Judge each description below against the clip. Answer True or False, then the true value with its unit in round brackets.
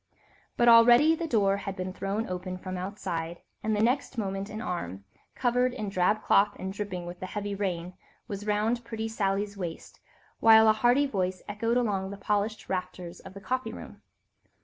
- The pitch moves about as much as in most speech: True (3.2 semitones)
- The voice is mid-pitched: False (205 Hz)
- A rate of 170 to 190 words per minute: True (180 wpm)